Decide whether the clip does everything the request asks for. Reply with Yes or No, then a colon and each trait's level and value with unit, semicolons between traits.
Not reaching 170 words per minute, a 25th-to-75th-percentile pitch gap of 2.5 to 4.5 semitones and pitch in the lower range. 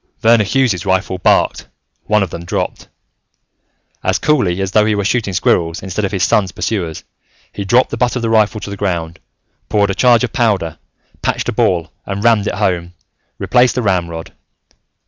No: average, 185 wpm; average, 4.0 semitones; low, 100 Hz